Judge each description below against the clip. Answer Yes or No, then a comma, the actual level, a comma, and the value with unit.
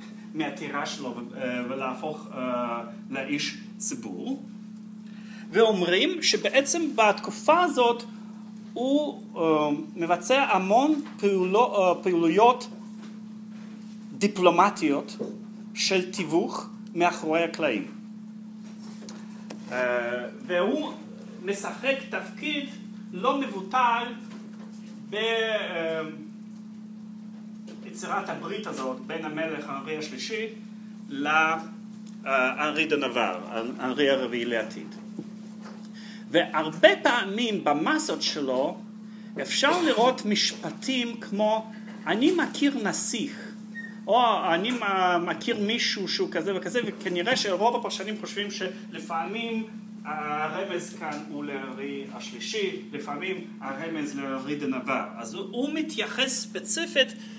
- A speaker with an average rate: No, slow, 75 wpm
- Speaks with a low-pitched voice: No, high, 215 Hz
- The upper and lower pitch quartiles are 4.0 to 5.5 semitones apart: No, average, 2.7 semitones